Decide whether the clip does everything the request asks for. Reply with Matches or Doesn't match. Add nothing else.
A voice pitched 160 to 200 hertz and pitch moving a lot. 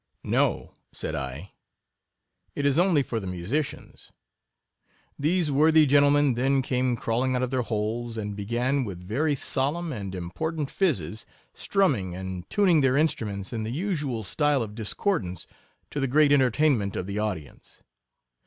Doesn't match